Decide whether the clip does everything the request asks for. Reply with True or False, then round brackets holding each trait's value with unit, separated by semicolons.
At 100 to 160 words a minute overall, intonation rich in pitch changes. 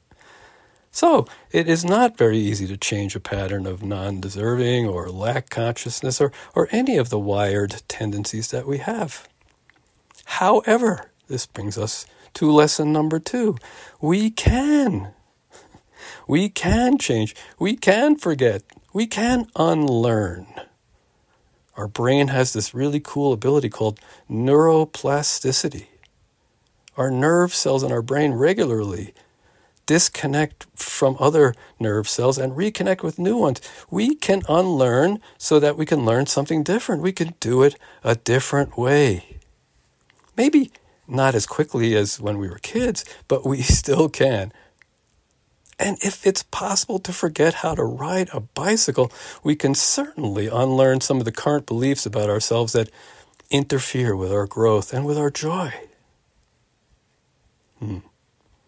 True (135 wpm; 7.6 semitones)